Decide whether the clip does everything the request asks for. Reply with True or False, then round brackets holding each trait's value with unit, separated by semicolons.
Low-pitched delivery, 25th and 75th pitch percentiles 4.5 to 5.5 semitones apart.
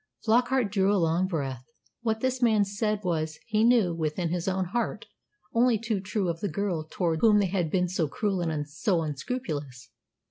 False (190 Hz; 5.0 semitones)